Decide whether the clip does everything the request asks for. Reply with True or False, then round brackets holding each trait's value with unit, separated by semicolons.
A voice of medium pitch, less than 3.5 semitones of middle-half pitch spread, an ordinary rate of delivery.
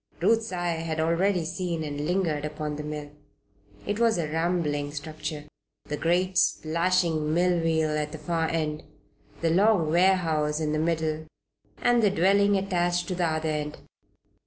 True (165 Hz; 2.8 semitones; 155 wpm)